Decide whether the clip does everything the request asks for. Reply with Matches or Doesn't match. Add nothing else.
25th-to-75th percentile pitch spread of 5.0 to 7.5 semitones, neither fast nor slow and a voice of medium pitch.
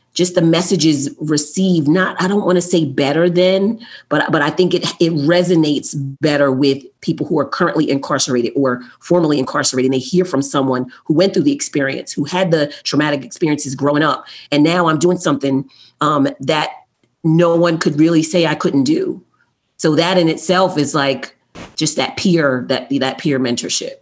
Doesn't match